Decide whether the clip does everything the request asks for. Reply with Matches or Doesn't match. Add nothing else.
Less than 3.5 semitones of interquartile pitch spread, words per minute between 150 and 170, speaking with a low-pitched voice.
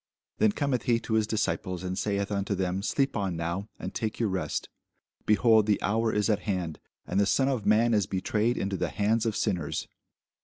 Doesn't match